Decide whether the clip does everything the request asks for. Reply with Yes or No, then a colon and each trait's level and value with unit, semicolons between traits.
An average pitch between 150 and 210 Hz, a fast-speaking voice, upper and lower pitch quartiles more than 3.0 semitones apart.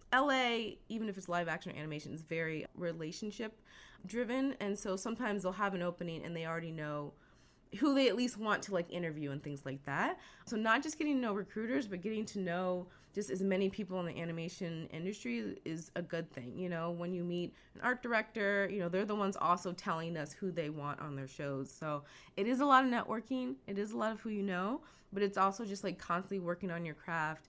Yes: medium, 185 Hz; fast, 230 wpm; average, 4.8 semitones